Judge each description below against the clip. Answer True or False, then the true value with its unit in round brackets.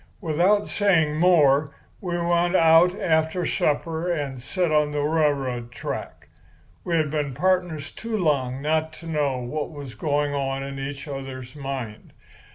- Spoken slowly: False (155 wpm)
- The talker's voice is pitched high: False (150 Hz)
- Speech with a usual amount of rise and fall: True (3.6 semitones)